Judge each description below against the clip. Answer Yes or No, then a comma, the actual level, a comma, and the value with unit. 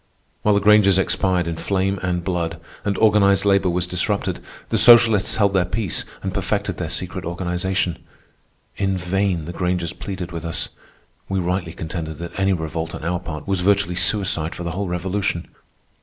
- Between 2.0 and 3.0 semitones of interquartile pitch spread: Yes, narrow, 2.4 semitones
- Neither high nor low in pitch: No, very low, 90 Hz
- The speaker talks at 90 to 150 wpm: No, average, 170 wpm